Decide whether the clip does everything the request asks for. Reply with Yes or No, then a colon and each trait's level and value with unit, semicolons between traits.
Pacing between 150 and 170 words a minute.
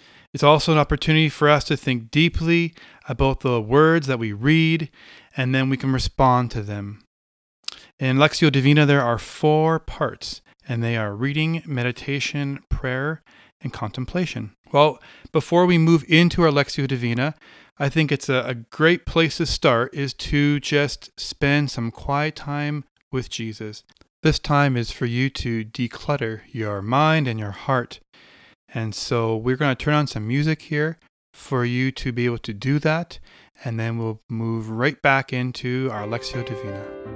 Yes: average, 165 wpm